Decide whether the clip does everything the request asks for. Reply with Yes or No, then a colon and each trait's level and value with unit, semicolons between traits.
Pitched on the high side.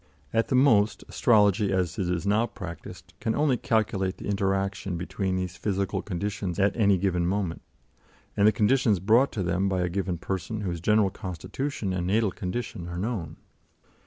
No: low, 100 Hz